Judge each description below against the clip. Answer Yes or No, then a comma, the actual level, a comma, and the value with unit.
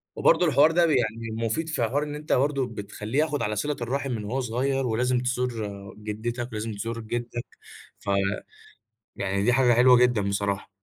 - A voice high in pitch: No, low, 120 Hz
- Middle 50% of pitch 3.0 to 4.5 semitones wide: Yes, average, 3.6 semitones